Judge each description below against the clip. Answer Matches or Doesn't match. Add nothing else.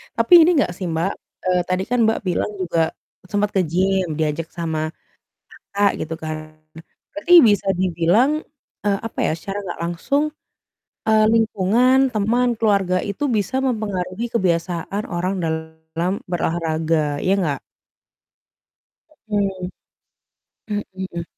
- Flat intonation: Doesn't match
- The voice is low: Doesn't match